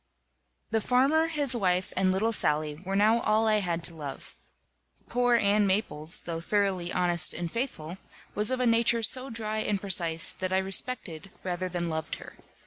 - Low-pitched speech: No, high, 195 Hz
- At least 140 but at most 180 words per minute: Yes, average, 175 wpm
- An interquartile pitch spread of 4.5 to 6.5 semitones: Yes, average, 4.8 semitones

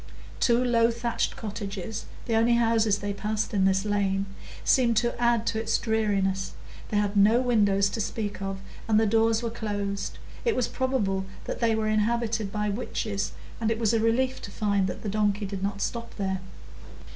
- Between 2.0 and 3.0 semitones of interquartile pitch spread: Yes, narrow, 2.5 semitones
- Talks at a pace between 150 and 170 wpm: No, average, 180 wpm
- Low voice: No, high, 215 Hz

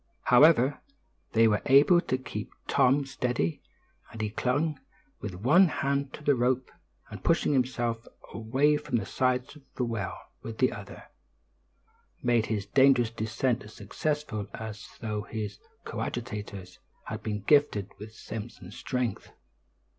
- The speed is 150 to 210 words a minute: No, average, 140 wpm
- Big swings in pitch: No, average, 3.9 semitones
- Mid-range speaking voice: No, low, 120 Hz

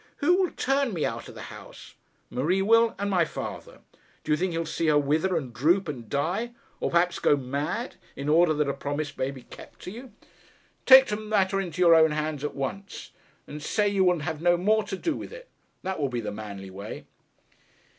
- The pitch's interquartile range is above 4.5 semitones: Yes, wide, 5.6 semitones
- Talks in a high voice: No, medium, 170 Hz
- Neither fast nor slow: No, fast, 215 wpm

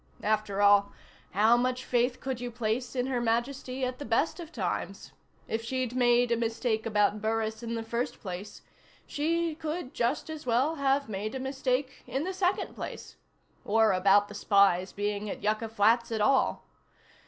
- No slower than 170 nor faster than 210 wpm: Yes, average, 175 wpm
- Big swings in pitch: No, average, 3.5 semitones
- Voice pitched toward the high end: Yes, high, 235 Hz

